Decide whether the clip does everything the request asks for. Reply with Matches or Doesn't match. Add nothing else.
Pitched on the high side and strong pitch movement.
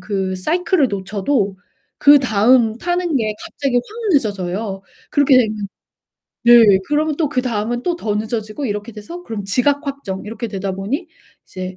Matches